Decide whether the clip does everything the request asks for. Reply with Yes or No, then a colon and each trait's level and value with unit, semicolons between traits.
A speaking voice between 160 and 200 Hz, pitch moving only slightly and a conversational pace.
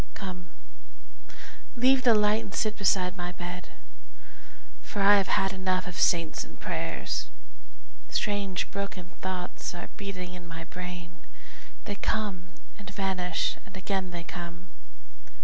No: medium, 185 Hz; narrow, 2.1 semitones; slow, 130 wpm